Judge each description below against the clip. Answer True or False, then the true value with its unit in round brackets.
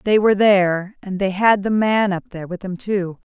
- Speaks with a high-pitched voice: True (195 Hz)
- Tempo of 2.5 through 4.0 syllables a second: False (5.5 syllables/s)